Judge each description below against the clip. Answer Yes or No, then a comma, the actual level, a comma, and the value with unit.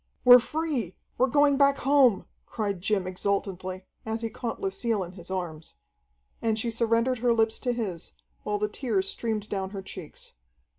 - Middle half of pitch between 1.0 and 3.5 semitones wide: No, average, 4.4 semitones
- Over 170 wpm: No, average, 165 wpm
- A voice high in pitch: Yes, high, 220 Hz